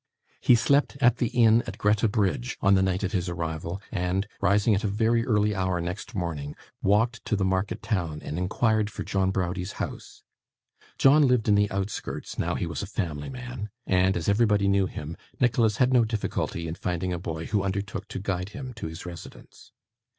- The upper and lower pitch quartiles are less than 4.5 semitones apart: Yes, average, 3.8 semitones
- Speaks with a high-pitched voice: No, low, 100 Hz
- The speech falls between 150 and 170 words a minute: No, average, 195 wpm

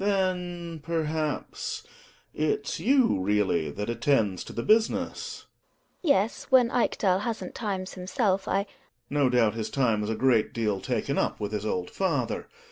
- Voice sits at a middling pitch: Yes, medium, 155 Hz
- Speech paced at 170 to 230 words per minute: No, average, 155 wpm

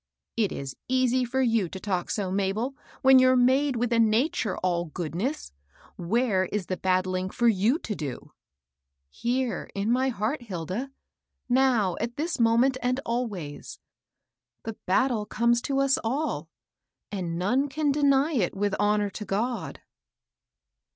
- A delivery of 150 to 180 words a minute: Yes, average, 155 wpm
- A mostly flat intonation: No, wide, 5.5 semitones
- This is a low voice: No, high, 225 Hz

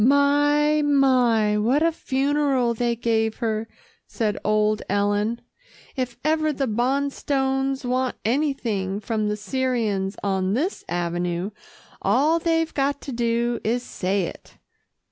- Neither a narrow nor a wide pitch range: Yes, average, 4.8 semitones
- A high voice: Yes, high, 240 Hz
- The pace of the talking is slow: Yes, slow, 125 wpm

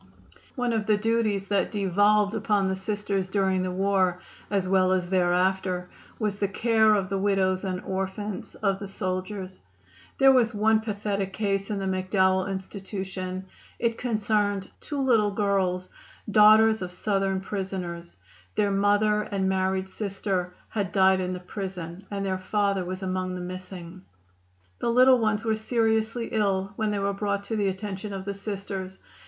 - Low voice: No, high, 195 Hz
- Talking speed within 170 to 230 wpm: No, average, 160 wpm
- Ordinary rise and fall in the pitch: No, narrow, 2.0 semitones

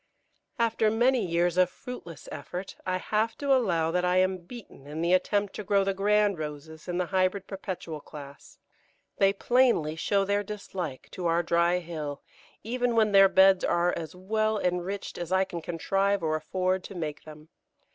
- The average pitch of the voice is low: No, medium, 185 Hz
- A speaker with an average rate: Yes, average, 180 wpm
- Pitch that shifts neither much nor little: Yes, average, 3.2 semitones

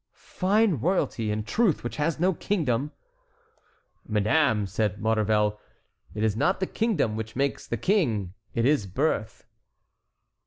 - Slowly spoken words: Yes, slow, 130 wpm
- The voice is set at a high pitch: No, low, 120 Hz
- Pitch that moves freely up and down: Yes, wide, 7.5 semitones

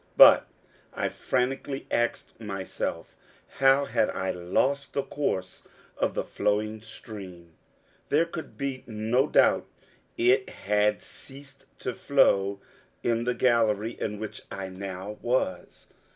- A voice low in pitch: Yes, low, 115 Hz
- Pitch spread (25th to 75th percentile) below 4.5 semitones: No, average, 5.1 semitones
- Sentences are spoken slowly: Yes, slow, 125 wpm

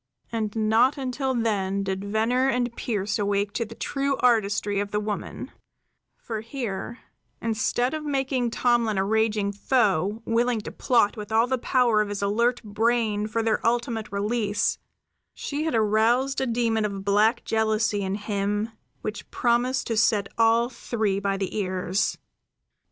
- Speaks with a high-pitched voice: Yes, high, 220 Hz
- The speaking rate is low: No, average, 155 wpm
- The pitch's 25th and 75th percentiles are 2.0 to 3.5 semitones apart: Yes, average, 2.8 semitones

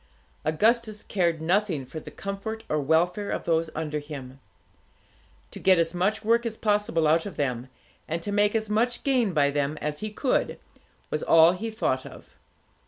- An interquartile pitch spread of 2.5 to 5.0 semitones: No, wide, 5.6 semitones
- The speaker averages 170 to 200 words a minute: Yes, average, 175 wpm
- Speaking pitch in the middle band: Yes, medium, 175 Hz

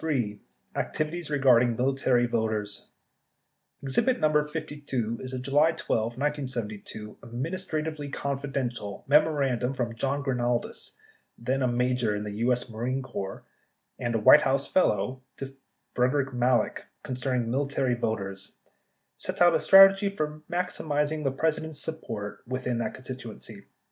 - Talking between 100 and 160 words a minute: Yes, slow, 135 wpm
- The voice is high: No, low, 130 Hz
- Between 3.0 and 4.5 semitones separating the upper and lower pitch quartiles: Yes, average, 3.8 semitones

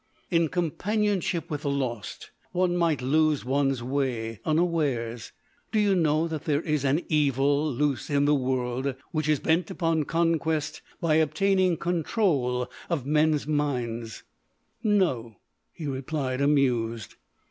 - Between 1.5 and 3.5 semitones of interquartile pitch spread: No, average, 4.0 semitones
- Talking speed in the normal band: No, slow, 125 wpm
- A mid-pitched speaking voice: Yes, medium, 150 Hz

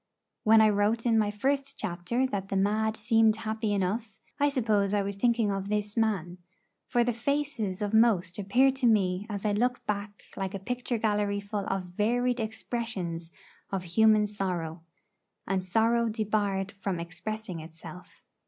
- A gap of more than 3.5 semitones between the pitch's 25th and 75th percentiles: No, average, 2.7 semitones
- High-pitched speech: Yes, high, 210 Hz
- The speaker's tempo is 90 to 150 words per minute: No, average, 160 wpm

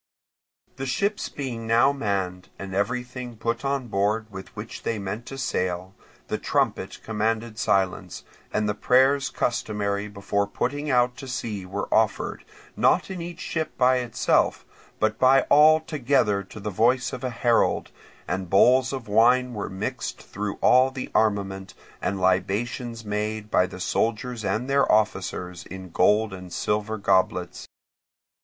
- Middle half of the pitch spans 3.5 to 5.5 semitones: Yes, average, 4.1 semitones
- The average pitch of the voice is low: Yes, low, 110 Hz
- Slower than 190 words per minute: Yes, average, 150 wpm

